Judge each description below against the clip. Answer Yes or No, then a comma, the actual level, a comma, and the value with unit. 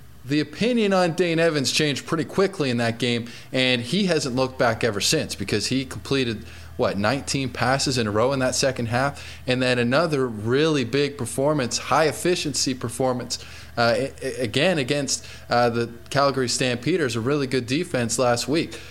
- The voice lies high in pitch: No, low, 130 Hz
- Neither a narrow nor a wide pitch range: Yes, average, 3.3 semitones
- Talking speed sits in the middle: Yes, average, 170 wpm